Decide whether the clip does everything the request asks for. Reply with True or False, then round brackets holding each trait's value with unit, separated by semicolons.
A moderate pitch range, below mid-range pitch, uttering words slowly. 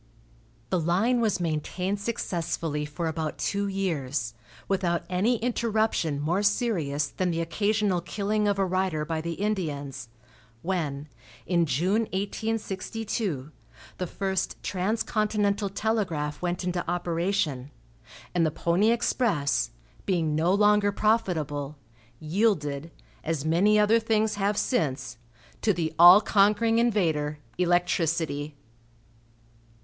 False (4.8 semitones; 180 Hz; 115 wpm)